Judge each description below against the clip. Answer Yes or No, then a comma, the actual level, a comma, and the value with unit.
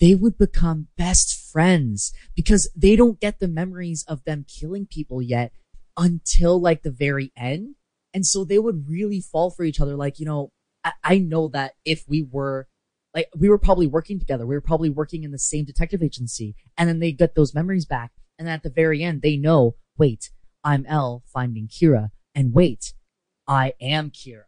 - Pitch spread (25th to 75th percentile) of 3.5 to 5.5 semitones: Yes, average, 4.1 semitones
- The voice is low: No, medium, 155 Hz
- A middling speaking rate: Yes, average, 195 wpm